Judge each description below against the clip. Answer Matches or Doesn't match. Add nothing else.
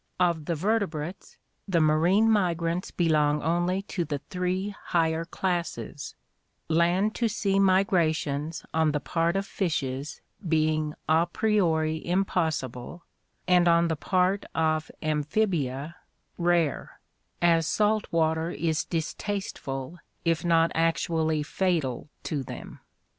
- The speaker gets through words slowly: Matches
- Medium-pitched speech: Matches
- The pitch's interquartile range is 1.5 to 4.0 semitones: Matches